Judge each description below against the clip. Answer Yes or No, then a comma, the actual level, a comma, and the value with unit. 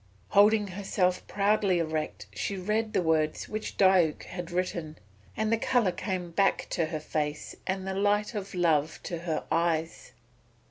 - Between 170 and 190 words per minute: No, average, 155 wpm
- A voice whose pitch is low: No, medium, 185 Hz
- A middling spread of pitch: Yes, average, 3.6 semitones